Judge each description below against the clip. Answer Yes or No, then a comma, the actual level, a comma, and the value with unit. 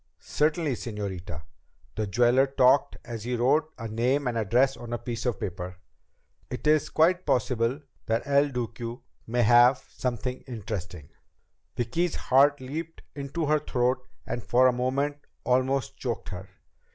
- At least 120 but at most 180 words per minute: Yes, average, 150 wpm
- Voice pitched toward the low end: Yes, low, 125 Hz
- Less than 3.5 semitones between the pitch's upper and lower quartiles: Yes, average, 3.1 semitones